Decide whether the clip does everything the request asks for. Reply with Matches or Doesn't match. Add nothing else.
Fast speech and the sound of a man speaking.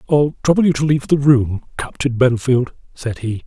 Doesn't match